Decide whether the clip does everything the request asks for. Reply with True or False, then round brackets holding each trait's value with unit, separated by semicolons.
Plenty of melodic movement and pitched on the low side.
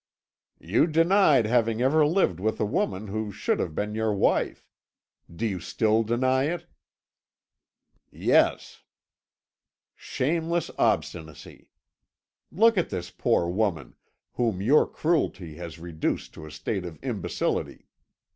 True (8.8 semitones; 110 Hz)